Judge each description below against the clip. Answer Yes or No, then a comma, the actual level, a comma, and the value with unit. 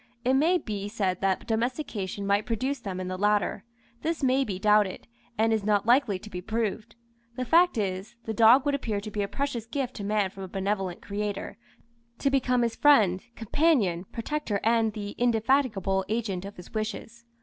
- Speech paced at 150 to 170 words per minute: No, average, 185 wpm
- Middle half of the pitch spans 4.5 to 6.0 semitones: No, average, 3.7 semitones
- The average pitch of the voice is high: Yes, high, 215 Hz